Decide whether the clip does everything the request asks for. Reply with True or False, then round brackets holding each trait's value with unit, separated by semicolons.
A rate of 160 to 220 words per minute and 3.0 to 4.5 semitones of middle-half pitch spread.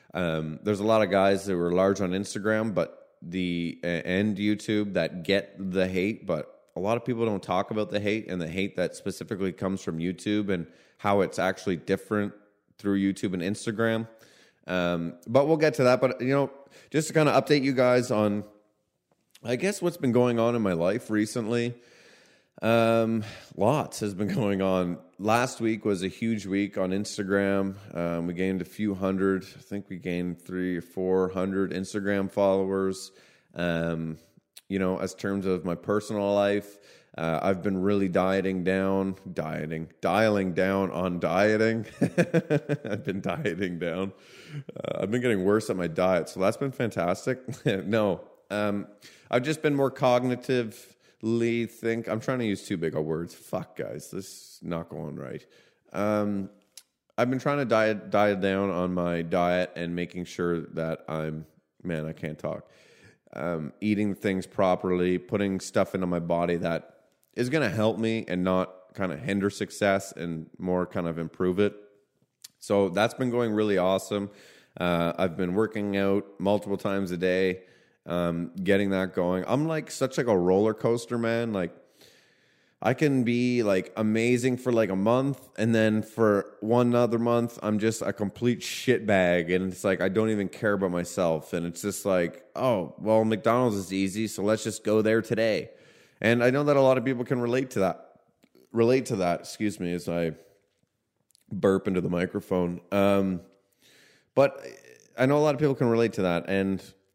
True (180 wpm; 3.5 semitones)